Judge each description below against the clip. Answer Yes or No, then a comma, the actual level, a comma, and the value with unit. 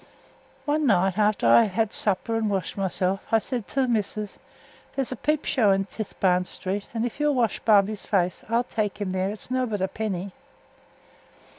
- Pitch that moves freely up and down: No, average, 3.3 semitones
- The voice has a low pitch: No, high, 210 Hz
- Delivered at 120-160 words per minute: No, average, 185 wpm